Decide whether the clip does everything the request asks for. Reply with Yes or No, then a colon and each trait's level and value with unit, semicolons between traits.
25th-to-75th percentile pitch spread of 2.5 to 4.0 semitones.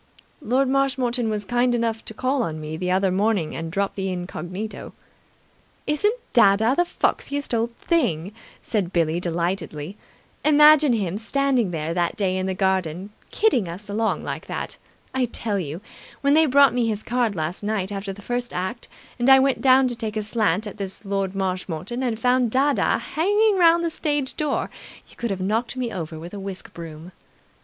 No: wide, 5.6 semitones